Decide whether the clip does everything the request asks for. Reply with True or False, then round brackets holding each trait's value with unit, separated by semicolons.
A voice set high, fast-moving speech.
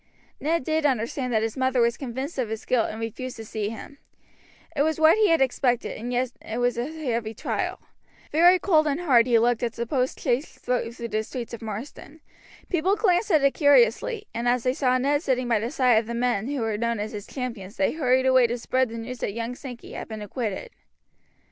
True (250 Hz; 220 wpm)